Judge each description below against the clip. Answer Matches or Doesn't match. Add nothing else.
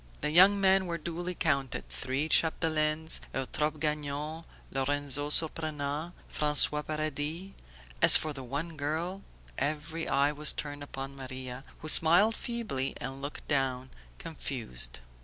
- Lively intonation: Doesn't match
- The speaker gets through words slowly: Matches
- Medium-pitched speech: Matches